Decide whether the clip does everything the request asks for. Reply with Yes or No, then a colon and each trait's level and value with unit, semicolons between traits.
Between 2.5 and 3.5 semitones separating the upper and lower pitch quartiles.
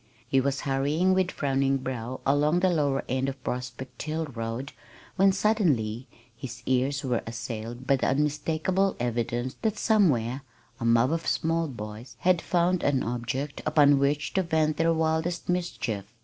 No: average, 4.7 semitones